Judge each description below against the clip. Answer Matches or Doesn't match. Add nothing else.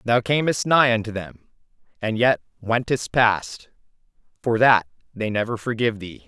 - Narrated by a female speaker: Doesn't match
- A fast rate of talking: Doesn't match